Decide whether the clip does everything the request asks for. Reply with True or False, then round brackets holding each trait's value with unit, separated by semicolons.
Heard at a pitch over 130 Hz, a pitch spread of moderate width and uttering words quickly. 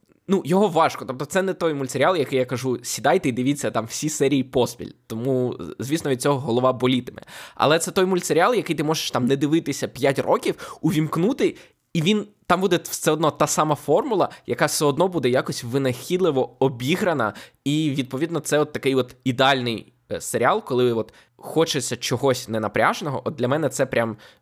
True (140 Hz; 4.3 semitones; 175 wpm)